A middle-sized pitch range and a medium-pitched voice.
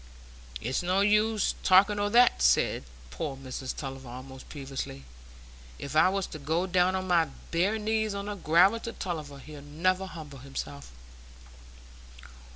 No: wide, 6.4 semitones; medium, 170 Hz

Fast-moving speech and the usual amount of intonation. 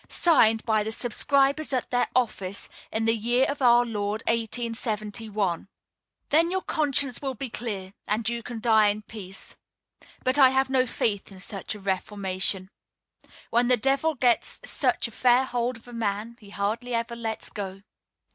No: average, 165 wpm; average, 3.3 semitones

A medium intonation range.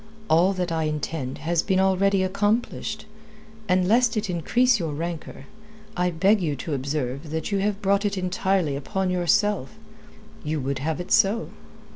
Yes: average, 4.1 semitones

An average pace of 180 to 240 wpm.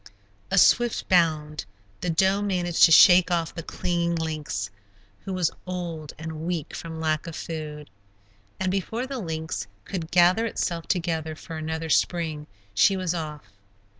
No: average, 150 wpm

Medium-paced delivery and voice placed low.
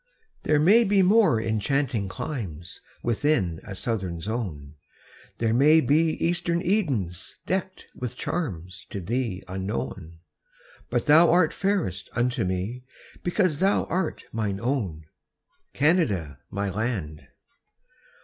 No: slow, 115 wpm; low, 120 Hz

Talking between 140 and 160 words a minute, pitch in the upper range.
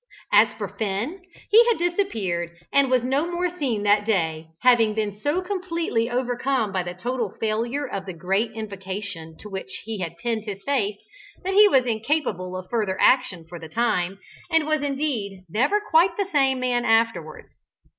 No: average, 175 wpm; high, 225 Hz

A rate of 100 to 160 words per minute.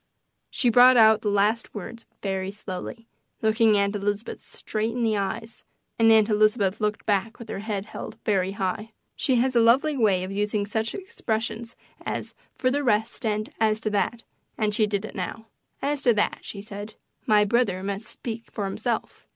No: average, 180 wpm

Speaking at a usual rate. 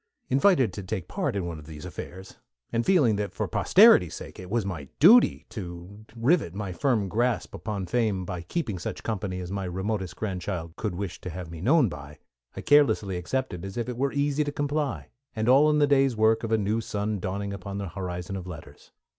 No: fast, 215 wpm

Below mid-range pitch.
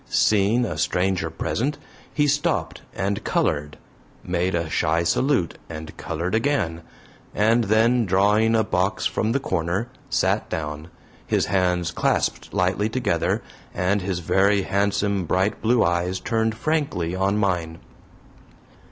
Yes: very low, 95 Hz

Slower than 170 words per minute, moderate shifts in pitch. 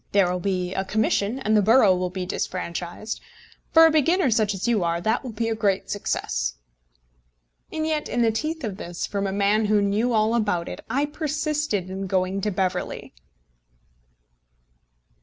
No: average, 175 wpm; average, 4.1 semitones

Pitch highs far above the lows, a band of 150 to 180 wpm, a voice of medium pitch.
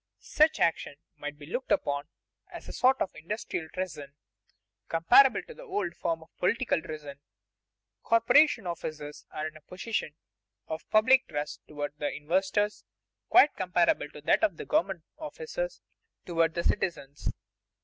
No: wide, 7.2 semitones; average, 140 wpm; medium, 170 Hz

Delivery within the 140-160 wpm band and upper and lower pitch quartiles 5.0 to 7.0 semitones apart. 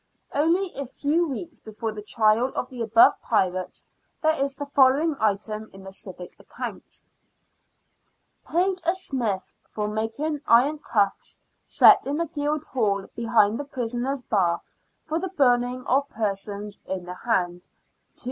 Yes: average, 150 wpm; wide, 5.6 semitones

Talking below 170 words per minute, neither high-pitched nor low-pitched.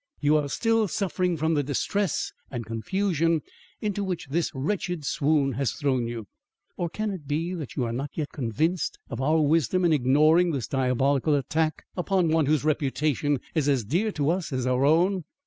No: average, 180 wpm; medium, 155 Hz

